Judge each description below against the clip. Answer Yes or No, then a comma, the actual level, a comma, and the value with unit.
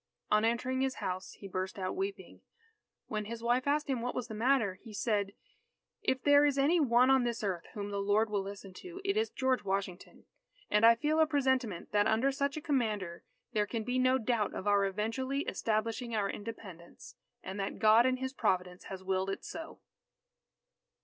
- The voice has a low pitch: No, high, 225 Hz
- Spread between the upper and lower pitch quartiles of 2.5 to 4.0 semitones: No, average, 4.6 semitones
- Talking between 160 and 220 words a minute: Yes, average, 195 wpm